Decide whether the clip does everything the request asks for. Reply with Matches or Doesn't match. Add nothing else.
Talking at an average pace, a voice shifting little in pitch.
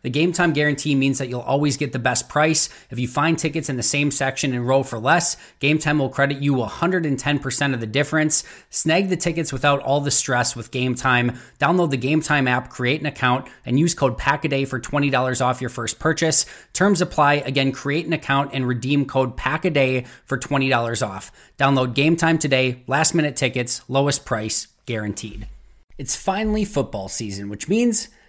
Doesn't match